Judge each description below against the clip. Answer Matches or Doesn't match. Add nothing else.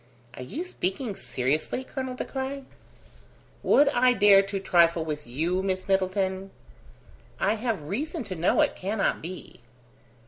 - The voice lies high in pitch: Matches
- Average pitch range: Doesn't match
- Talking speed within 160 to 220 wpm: Doesn't match